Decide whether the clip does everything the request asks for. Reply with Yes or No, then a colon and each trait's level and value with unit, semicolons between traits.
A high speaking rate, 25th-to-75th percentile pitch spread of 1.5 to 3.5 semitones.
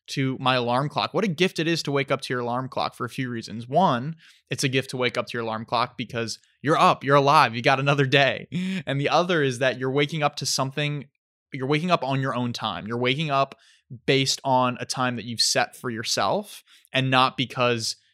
Yes: fast, 240 wpm; narrow, 2.6 semitones